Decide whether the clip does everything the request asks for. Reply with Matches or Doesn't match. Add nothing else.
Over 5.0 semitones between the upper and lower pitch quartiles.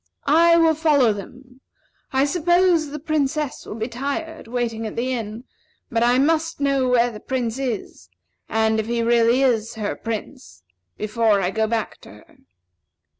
Doesn't match